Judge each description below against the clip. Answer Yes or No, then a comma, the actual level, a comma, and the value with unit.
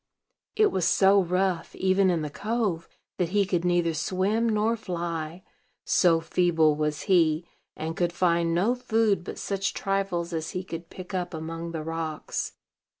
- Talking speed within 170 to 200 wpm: No, average, 160 wpm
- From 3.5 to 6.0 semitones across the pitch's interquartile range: No, average, 2.9 semitones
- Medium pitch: Yes, medium, 175 Hz